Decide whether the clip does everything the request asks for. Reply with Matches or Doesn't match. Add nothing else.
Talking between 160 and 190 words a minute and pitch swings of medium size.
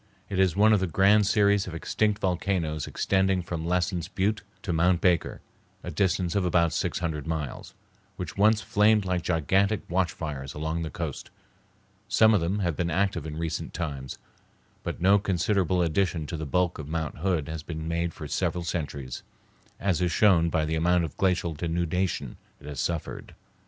Matches